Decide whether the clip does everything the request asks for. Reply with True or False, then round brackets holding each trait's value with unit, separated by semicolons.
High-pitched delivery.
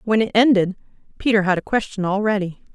True (205 Hz)